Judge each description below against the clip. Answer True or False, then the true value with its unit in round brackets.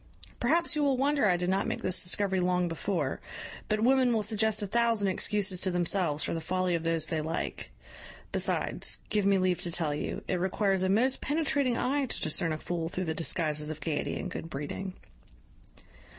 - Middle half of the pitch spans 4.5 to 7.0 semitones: True (4.8 semitones)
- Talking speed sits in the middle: True (195 wpm)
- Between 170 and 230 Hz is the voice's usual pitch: True (185 Hz)